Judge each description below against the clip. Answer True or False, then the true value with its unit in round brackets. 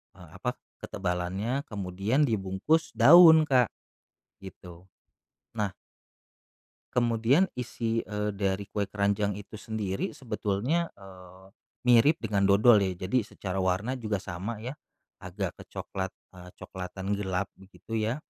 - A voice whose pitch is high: False (105 Hz)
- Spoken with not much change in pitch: False (3.7 semitones)